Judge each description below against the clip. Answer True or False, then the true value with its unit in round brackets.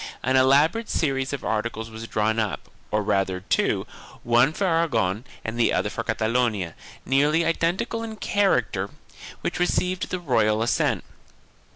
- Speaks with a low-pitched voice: True (125 Hz)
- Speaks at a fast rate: False (150 wpm)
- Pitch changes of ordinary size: False (7.1 semitones)